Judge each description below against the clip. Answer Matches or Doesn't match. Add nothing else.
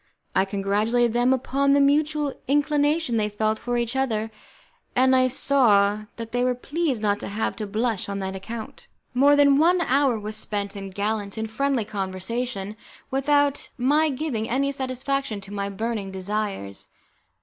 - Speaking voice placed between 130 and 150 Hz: Doesn't match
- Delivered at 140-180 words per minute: Matches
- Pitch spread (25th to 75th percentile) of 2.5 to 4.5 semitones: Doesn't match